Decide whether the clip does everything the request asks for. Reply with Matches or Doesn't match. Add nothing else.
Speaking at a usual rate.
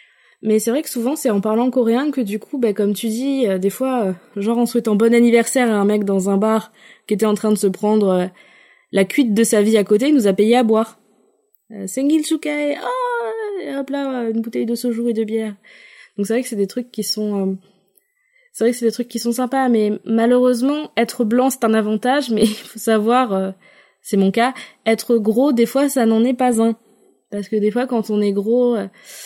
Doesn't match